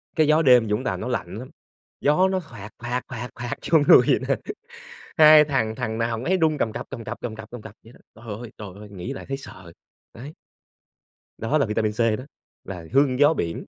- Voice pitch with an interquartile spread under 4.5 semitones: No, average, 4.9 semitones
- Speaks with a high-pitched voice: No, low, 120 Hz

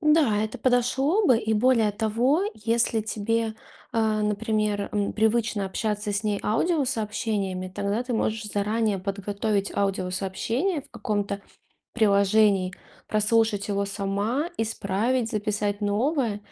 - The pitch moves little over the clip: Yes, narrow, 2.3 semitones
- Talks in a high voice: Yes, high, 215 Hz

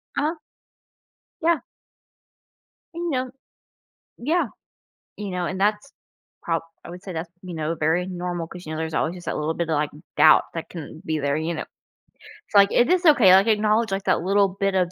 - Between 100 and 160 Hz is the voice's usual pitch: No, medium, 185 Hz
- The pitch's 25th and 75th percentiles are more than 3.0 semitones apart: Yes, average, 4.5 semitones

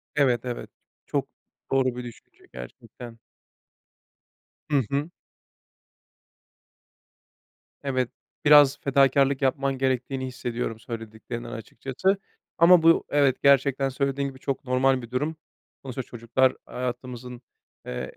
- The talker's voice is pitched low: Yes, low, 130 Hz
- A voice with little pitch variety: Yes, narrow, 2.1 semitones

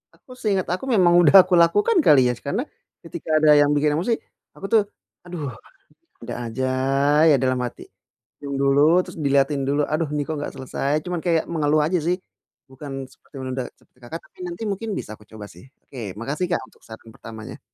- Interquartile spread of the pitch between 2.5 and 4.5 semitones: No, average, 5.0 semitones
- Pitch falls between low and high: Yes, medium, 150 Hz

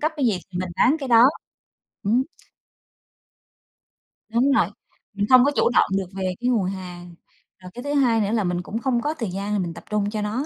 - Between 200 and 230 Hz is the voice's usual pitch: Yes, high, 215 Hz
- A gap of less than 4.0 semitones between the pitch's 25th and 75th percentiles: No, average, 5.0 semitones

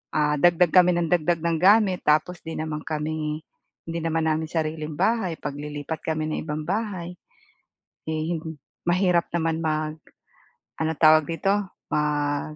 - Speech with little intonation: Yes, narrow, 2.1 semitones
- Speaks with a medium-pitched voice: Yes, medium, 160 Hz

